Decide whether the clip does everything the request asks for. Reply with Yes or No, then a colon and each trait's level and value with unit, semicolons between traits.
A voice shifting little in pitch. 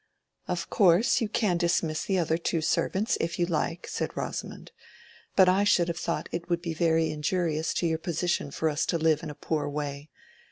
Yes: narrow, 2.1 semitones